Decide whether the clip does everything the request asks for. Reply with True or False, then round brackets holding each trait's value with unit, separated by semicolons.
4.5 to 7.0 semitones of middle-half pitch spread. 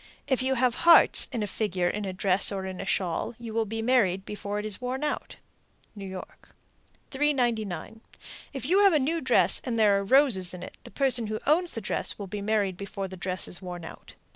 True (5.1 semitones)